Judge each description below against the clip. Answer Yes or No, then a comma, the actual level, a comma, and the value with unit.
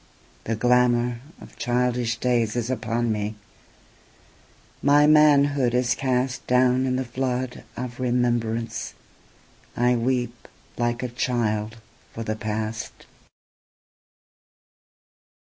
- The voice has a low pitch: Yes, low, 120 Hz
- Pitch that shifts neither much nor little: No, narrow, 1.7 semitones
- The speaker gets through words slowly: Yes, slow, 90 wpm